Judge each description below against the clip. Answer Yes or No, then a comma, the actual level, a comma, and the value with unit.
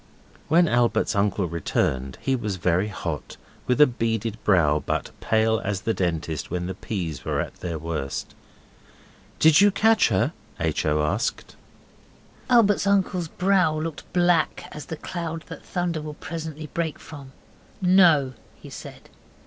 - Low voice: Yes, low, 125 Hz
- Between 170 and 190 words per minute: No, average, 150 wpm